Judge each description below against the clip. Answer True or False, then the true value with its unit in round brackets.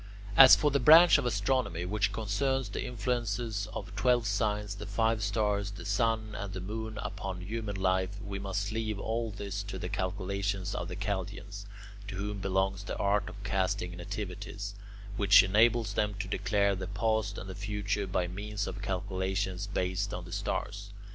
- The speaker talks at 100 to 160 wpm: False (175 wpm)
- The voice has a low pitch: True (100 Hz)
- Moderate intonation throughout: False (2.0 semitones)